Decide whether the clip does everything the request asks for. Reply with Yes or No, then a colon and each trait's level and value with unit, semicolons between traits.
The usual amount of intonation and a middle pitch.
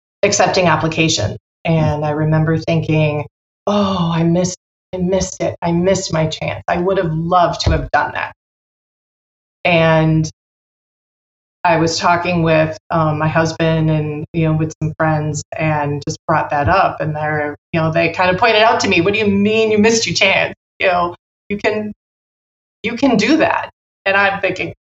Yes: average, 3.3 semitones; medium, 165 Hz